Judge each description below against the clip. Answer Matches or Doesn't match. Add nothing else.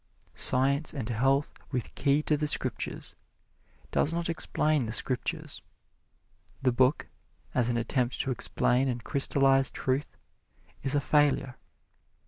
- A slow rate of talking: Matches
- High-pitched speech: Doesn't match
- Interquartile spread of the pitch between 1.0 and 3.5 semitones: Matches